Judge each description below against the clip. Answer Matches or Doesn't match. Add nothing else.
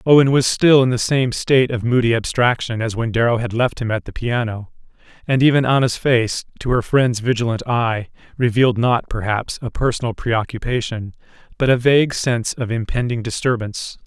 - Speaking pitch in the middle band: Doesn't match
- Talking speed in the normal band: Matches